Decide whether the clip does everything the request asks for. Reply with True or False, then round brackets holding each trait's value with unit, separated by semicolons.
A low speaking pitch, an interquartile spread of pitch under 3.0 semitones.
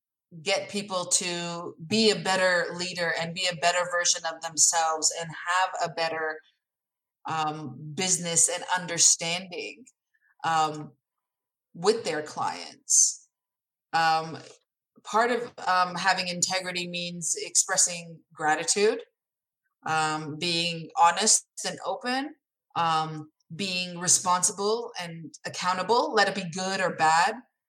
False (175 Hz; 2.6 semitones)